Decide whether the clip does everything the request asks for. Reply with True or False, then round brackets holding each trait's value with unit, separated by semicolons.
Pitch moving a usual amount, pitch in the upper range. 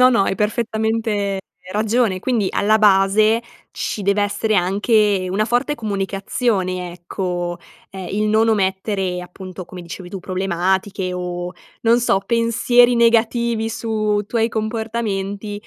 True (3.0 semitones; 205 Hz)